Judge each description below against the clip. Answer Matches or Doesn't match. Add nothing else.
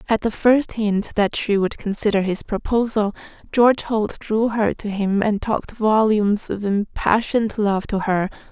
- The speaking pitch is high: Matches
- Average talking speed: Matches